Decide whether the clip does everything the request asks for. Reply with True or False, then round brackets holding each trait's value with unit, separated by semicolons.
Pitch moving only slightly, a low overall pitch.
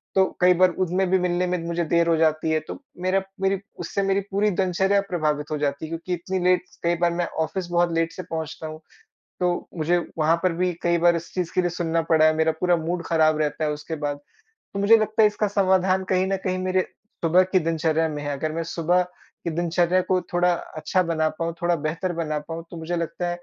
False (2.3 semitones; 175 Hz)